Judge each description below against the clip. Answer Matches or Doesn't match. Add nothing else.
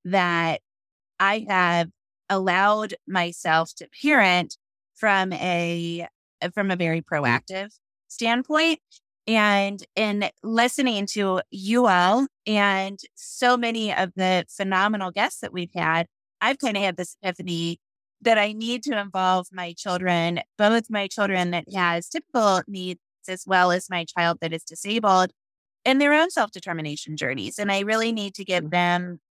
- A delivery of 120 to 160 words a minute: Matches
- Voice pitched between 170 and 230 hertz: Matches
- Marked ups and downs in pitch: Doesn't match